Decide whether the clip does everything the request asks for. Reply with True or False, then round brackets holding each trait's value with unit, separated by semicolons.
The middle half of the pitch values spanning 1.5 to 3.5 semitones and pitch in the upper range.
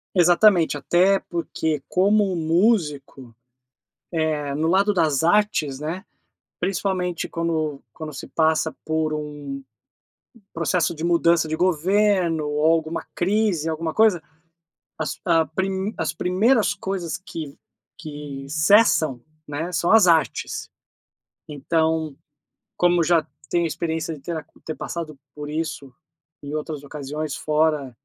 False (2.9 semitones; 160 Hz)